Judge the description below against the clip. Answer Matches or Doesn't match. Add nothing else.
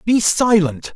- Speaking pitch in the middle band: Doesn't match